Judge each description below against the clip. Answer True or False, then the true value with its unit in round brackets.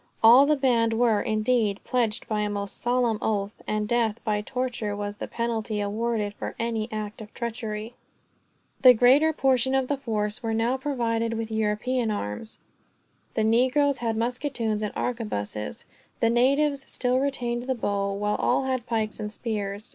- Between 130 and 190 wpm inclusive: True (160 wpm)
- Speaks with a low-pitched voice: False (230 Hz)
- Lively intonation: False (2.9 semitones)